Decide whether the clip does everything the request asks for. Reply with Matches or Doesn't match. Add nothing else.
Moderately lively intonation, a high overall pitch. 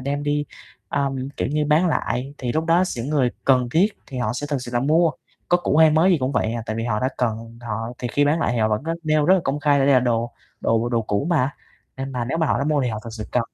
Doesn't match